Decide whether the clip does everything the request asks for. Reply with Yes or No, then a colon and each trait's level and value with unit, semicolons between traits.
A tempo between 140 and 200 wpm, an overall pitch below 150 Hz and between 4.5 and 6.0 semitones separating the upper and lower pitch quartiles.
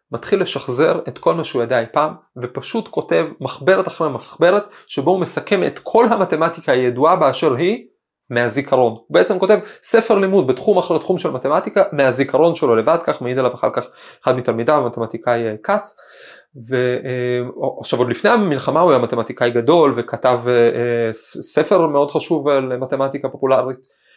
Yes: fast, 150 wpm; low, 135 Hz; average, 5.0 semitones